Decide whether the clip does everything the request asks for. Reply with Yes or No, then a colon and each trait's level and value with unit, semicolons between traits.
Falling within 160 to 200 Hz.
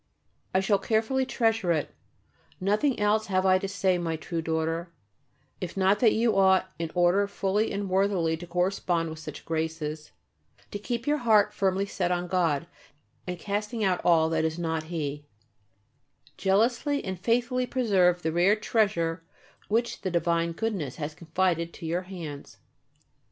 Yes: medium, 185 Hz